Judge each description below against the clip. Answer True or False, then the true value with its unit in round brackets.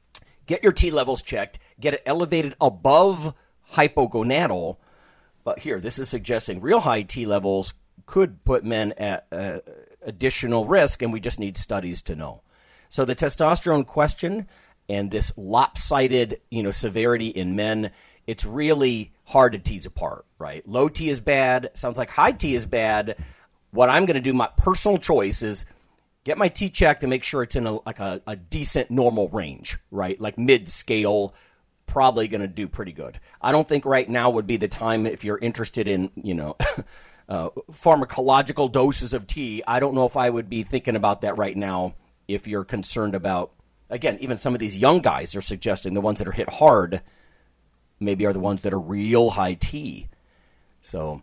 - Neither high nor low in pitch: False (115 Hz)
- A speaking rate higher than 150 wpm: True (185 wpm)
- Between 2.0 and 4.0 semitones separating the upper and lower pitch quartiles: False (4.9 semitones)